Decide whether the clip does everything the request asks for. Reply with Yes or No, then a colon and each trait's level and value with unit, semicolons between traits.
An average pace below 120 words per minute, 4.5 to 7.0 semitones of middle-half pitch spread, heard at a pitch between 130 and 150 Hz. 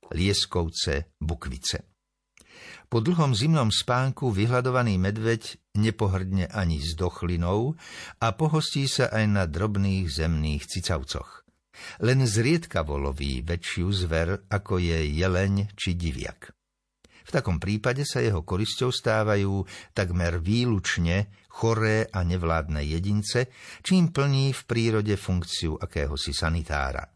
No: slow, 110 wpm; average, 5.1 semitones; low, 100 Hz